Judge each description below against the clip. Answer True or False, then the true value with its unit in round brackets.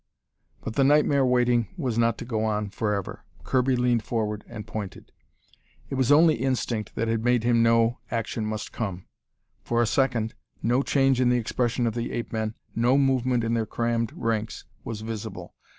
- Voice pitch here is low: True (115 Hz)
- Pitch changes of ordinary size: False (2.1 semitones)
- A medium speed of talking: True (180 wpm)